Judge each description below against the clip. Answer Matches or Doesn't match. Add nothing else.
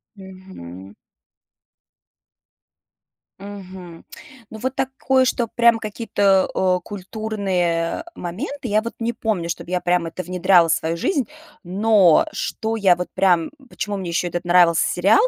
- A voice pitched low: Doesn't match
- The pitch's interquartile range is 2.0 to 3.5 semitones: Doesn't match